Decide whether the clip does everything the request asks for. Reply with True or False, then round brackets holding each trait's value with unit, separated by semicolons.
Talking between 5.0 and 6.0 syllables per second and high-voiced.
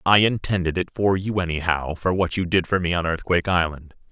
False (5.9 syllables/s; 90 Hz)